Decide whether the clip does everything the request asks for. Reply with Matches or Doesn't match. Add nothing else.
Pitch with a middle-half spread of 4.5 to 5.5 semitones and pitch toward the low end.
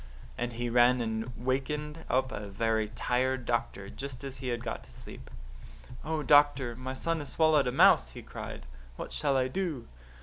Doesn't match